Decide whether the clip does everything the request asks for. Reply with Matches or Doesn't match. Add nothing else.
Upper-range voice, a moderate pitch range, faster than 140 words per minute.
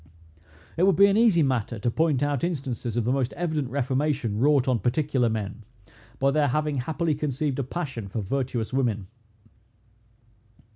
Doesn't match